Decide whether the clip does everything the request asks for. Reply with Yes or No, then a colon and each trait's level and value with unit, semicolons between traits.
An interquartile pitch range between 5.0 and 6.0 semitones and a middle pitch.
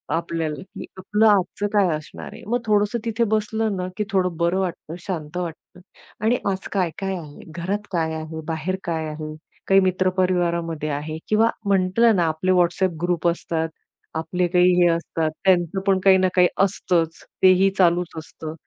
No: average, 2.8 semitones; medium, 180 Hz